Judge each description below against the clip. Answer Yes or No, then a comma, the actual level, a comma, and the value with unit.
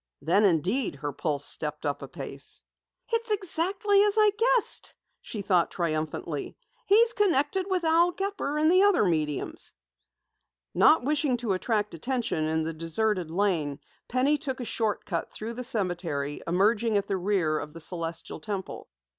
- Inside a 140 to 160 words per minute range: Yes, average, 155 wpm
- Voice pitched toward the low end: No, high, 210 Hz